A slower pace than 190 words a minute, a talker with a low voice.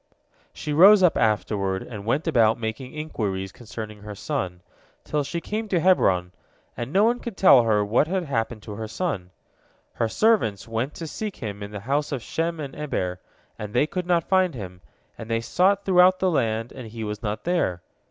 No: average, 195 wpm; low, 120 Hz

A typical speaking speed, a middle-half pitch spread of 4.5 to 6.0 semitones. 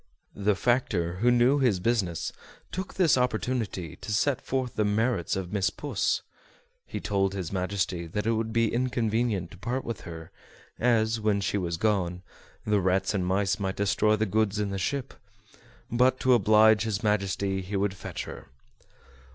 No: average, 170 wpm; average, 3.5 semitones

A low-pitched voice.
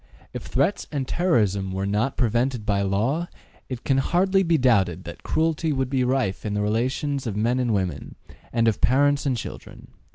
Yes: low, 125 Hz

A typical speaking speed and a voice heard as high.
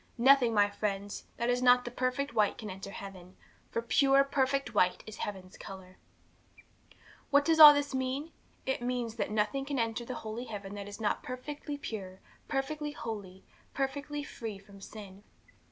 Yes: average, 165 wpm; high, 235 Hz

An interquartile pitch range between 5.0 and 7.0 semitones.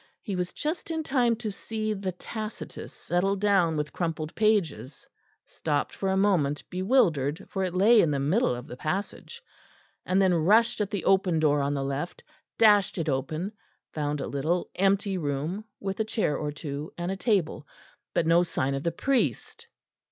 Yes: wide, 5.5 semitones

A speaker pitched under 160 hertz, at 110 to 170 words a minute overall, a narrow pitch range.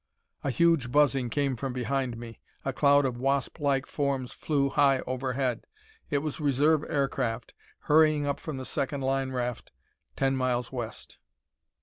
Yes: low, 135 Hz; average, 145 wpm; narrow, 2.1 semitones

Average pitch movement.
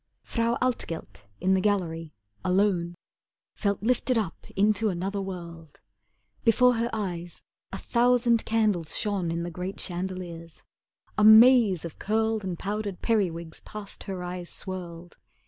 Yes: average, 4.0 semitones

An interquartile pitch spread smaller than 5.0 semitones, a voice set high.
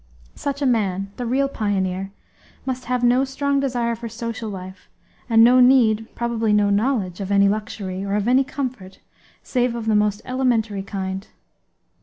Yes: average, 4.0 semitones; high, 225 Hz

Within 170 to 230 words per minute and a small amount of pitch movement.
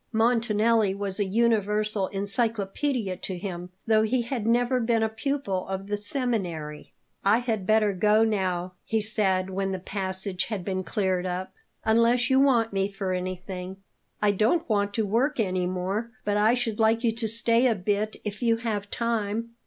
No: average, 175 wpm; average, 3.2 semitones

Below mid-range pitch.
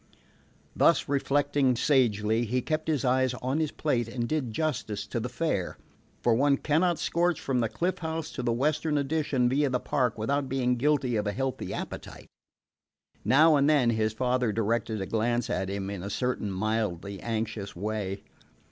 Yes: low, 125 Hz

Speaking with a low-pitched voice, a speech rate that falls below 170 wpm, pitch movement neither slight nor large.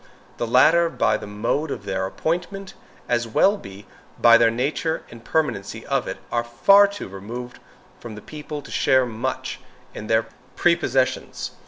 No: low, 120 Hz; average, 160 wpm; wide, 6.0 semitones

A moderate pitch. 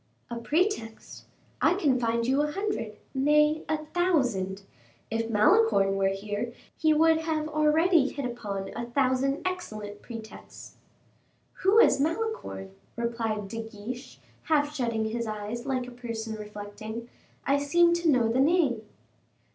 No: very high, 250 Hz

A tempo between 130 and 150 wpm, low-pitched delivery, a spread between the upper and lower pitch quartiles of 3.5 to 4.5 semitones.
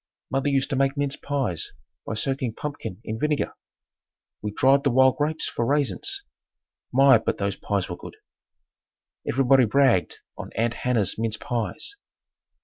Yes: average, 145 wpm; low, 130 Hz; average, 4.0 semitones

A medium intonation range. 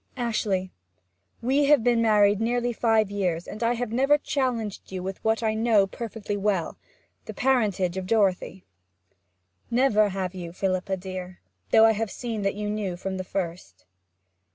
Yes: average, 3.4 semitones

